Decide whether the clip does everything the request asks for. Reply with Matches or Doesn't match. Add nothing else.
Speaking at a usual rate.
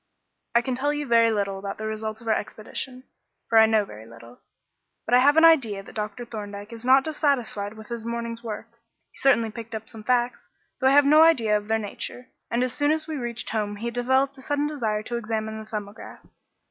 Doesn't match